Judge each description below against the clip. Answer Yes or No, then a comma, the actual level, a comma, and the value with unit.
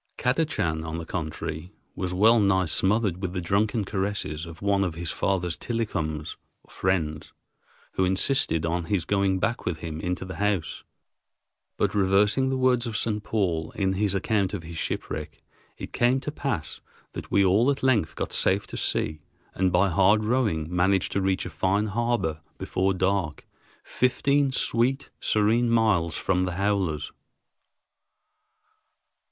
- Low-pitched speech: Yes, very low, 95 Hz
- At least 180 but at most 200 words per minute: No, average, 155 wpm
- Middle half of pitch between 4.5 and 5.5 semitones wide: No, average, 4.0 semitones